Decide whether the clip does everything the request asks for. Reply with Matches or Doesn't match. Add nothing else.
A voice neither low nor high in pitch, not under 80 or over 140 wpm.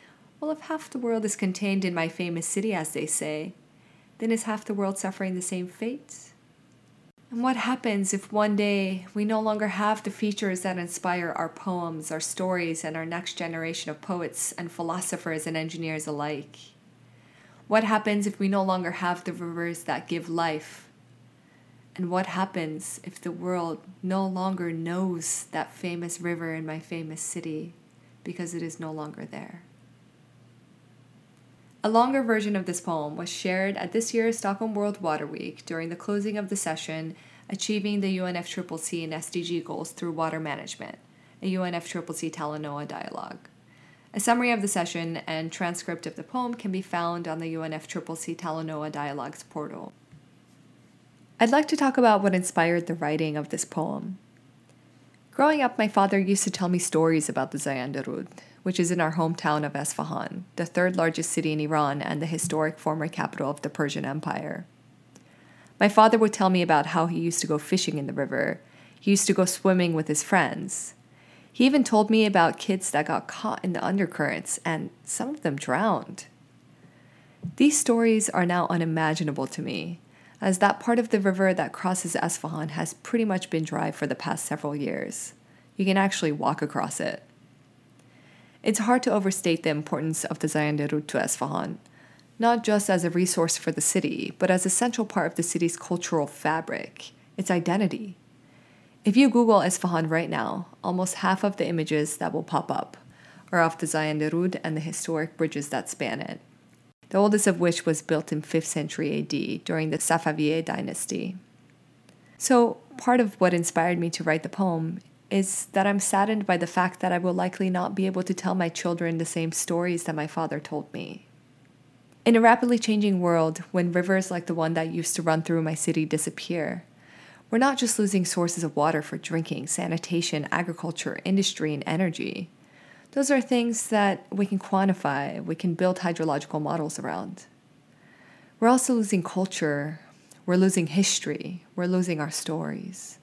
Doesn't match